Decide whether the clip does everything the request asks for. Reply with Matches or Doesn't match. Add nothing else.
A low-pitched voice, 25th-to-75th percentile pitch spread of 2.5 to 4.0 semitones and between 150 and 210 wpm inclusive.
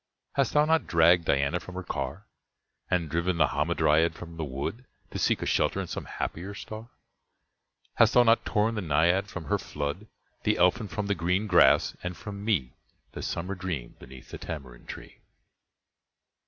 Doesn't match